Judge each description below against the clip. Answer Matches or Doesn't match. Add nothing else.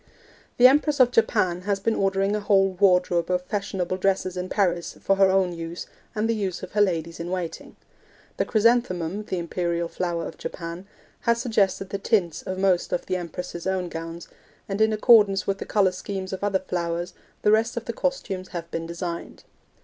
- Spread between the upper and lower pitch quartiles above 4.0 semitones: Doesn't match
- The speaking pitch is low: Doesn't match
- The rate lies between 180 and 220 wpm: Matches